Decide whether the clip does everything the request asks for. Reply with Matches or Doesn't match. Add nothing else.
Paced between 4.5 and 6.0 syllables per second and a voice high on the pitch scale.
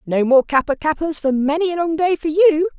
Matches